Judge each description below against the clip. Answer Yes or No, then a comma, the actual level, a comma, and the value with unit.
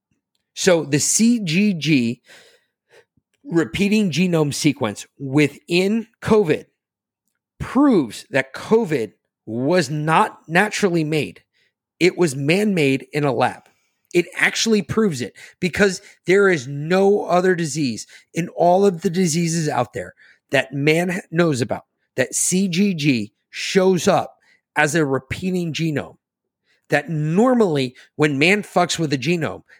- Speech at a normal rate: No, slow, 120 wpm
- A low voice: No, medium, 170 Hz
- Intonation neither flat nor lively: Yes, average, 4.7 semitones